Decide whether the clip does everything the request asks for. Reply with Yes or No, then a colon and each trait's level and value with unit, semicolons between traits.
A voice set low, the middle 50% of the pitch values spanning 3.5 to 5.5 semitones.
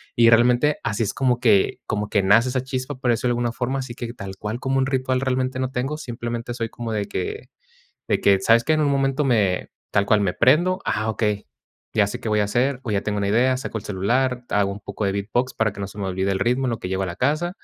Yes: low, 120 Hz; average, 4.0 semitones